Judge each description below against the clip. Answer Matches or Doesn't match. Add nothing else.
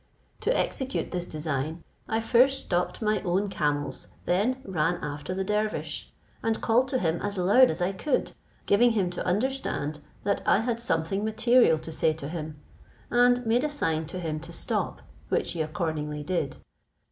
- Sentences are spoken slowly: Doesn't match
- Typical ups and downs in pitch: Doesn't match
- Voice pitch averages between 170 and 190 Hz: Matches